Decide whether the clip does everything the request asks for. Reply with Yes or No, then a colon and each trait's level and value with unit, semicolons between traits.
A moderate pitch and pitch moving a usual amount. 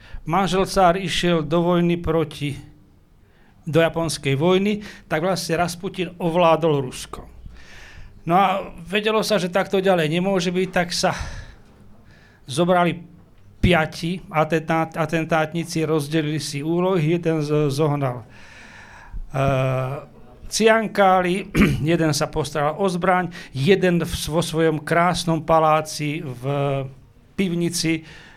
Yes: medium, 165 Hz; average, 3.1 semitones